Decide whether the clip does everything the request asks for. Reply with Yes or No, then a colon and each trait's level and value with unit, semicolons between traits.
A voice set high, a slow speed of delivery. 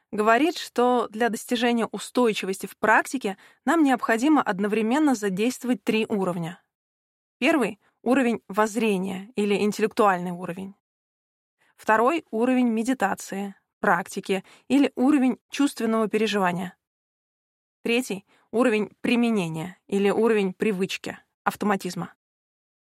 Yes: high, 220 Hz; slow, 90 wpm